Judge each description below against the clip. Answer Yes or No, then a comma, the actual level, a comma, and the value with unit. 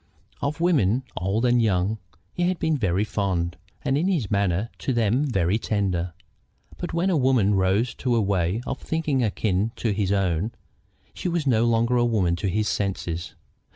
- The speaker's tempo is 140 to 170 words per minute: No, average, 180 wpm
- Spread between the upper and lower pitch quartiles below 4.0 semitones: No, average, 5.2 semitones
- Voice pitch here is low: Yes, low, 110 Hz